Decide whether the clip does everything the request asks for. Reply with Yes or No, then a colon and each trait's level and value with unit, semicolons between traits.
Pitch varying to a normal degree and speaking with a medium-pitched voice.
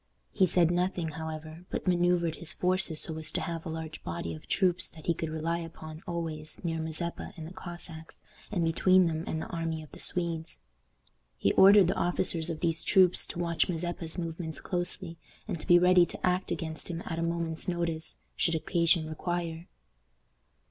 No: narrow, 1.7 semitones; medium, 165 Hz